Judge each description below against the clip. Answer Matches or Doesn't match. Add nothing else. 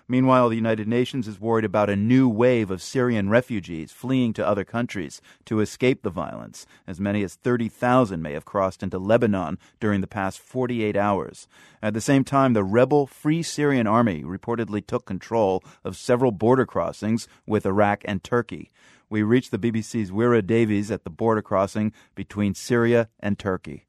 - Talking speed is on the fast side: Doesn't match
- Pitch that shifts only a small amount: Doesn't match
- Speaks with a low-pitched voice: Matches